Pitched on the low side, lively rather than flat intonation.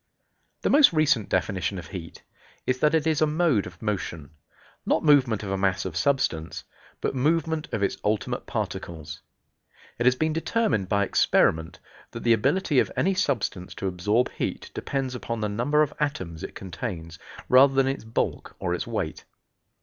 Yes: low, 115 Hz; wide, 7.7 semitones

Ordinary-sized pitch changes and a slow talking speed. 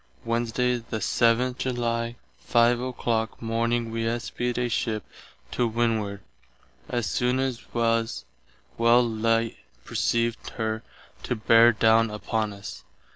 No: narrow, 1.1 semitones; slow, 125 wpm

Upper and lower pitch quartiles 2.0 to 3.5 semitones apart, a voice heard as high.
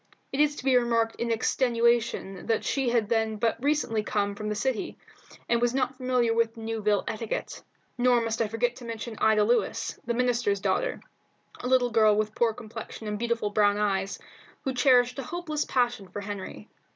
Yes: narrow, 2.6 semitones; high, 230 Hz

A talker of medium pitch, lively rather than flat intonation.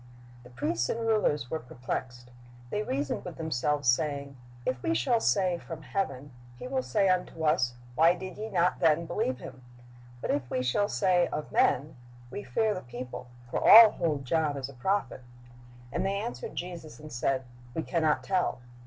Yes: medium, 155 Hz; wide, 6.3 semitones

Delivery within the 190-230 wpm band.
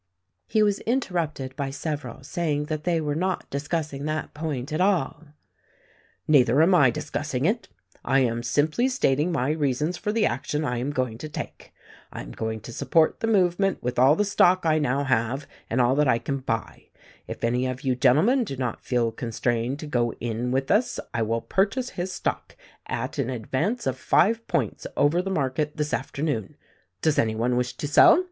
Yes: average, 195 wpm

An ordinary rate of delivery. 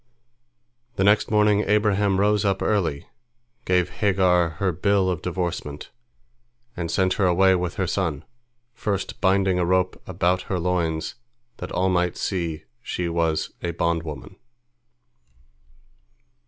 No: slow, 125 wpm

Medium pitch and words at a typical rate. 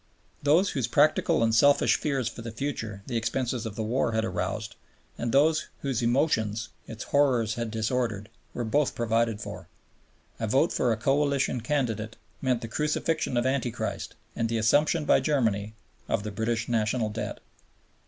No: low, 115 Hz; average, 165 wpm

